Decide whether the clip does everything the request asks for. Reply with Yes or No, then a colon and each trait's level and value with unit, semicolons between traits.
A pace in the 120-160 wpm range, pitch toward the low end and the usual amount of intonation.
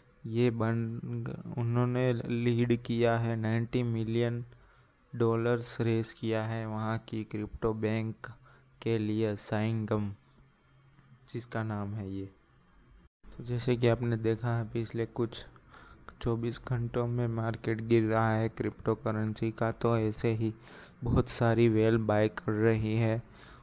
No: average, 130 wpm; low, 115 Hz; narrow, 1.2 semitones